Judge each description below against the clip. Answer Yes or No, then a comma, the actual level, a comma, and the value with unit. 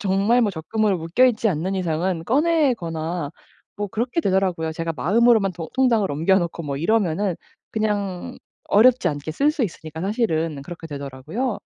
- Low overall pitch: No, high, 190 Hz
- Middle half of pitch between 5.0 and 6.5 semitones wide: Yes, wide, 5.5 semitones